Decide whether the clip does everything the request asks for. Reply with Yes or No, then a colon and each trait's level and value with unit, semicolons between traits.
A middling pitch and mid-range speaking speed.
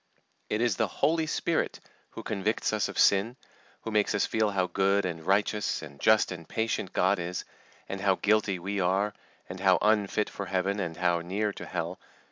No: low, 100 Hz; average, 190 wpm